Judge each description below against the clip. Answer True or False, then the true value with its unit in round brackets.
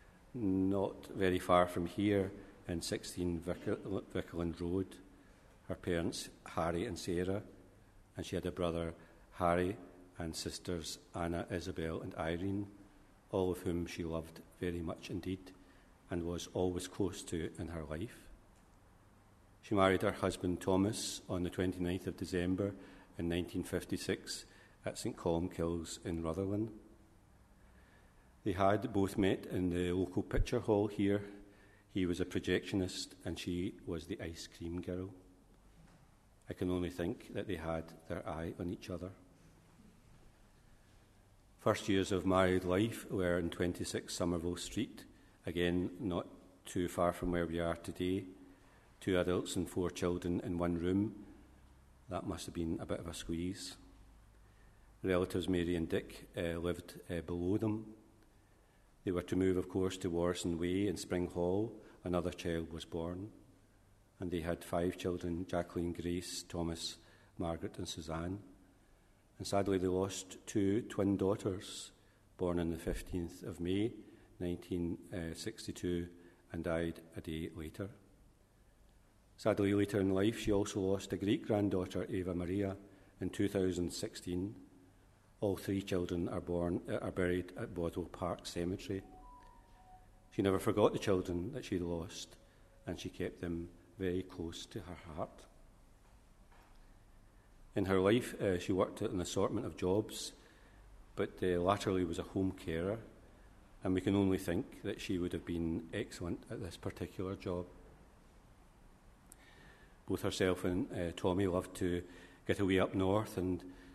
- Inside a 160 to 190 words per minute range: False (145 wpm)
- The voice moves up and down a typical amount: False (2.2 semitones)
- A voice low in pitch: True (95 Hz)